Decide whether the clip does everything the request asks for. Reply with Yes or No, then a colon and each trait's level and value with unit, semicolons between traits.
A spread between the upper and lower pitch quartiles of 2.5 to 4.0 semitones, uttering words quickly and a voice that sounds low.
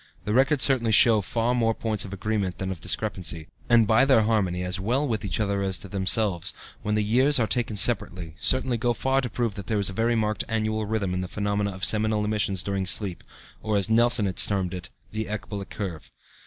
Yes: average, 2.8 semitones; fast, 220 wpm; low, 105 Hz